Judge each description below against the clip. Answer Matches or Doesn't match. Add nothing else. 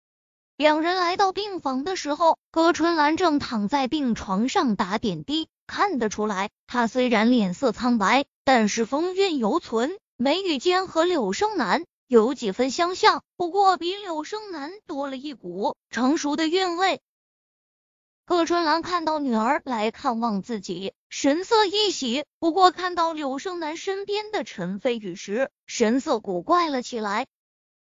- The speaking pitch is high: Matches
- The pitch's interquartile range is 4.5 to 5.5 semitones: Doesn't match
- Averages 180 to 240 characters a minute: Matches